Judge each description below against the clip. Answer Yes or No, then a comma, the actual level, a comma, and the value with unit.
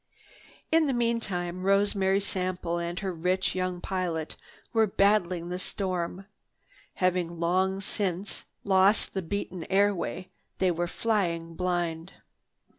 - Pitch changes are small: Yes, narrow, 2.2 semitones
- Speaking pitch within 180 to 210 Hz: Yes, medium, 185 Hz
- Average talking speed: No, slow, 115 wpm